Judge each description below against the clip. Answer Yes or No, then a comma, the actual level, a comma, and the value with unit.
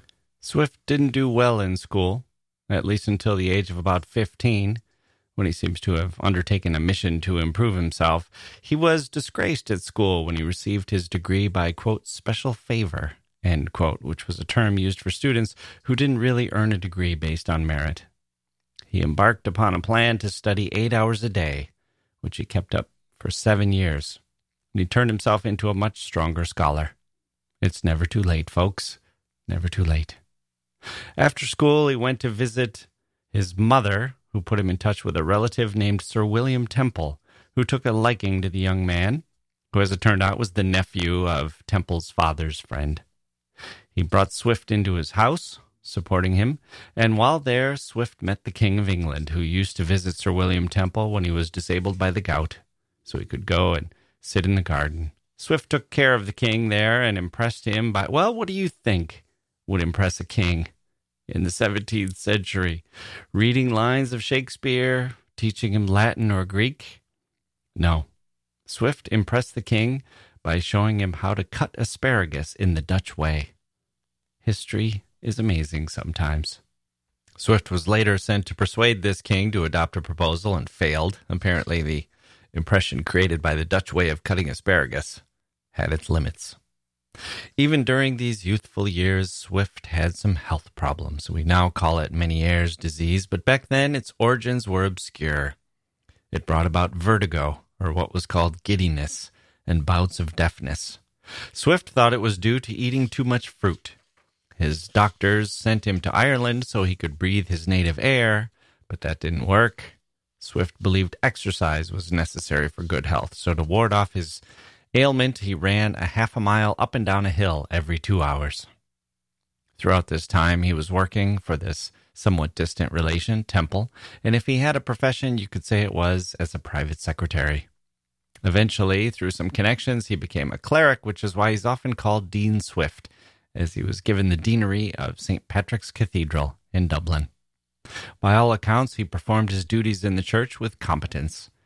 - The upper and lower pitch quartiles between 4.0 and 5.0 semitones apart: Yes, average, 4.6 semitones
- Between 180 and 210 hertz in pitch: No, very low, 95 Hz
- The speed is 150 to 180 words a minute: Yes, average, 175 wpm